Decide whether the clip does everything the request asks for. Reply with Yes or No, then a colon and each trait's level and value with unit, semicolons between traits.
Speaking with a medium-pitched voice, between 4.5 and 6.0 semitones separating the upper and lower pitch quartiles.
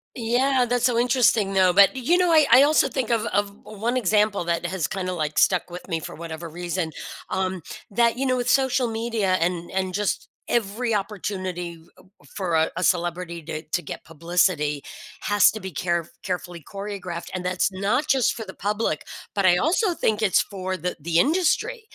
No: high, 195 Hz; average, 5.1 semitones